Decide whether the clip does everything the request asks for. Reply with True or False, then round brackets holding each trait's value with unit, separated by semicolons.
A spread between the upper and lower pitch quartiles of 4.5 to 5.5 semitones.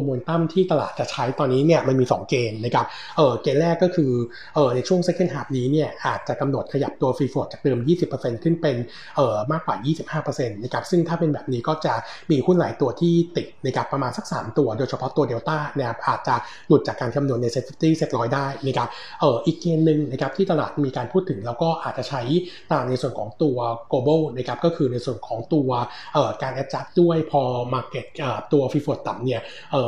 False (4.0 semitones)